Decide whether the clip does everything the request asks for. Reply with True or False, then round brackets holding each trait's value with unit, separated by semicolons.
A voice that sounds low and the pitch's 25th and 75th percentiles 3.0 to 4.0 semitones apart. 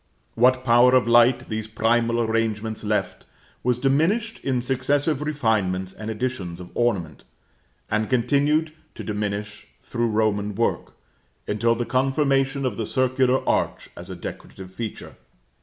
True (120 Hz; 3.6 semitones)